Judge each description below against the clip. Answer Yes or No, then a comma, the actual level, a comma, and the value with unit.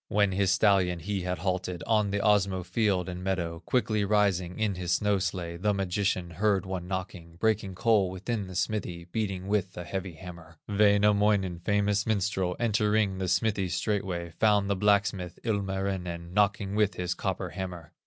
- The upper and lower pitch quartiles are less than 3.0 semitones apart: Yes, narrow, 2.4 semitones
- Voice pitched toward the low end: Yes, very low, 95 Hz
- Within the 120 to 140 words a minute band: No, average, 165 wpm